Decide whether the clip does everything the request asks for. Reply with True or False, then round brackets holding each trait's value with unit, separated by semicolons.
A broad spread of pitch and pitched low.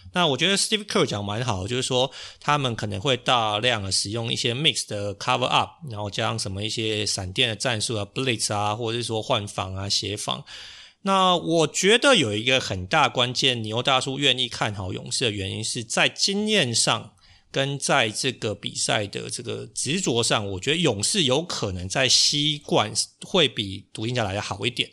False (4.4 semitones; 120 Hz)